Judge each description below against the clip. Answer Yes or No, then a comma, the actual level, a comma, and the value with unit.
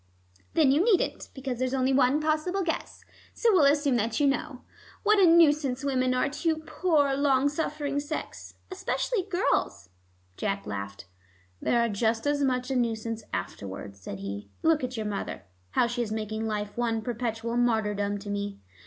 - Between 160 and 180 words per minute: Yes, average, 170 wpm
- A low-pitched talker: No, very high, 255 Hz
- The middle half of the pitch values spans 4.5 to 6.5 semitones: Yes, average, 5.2 semitones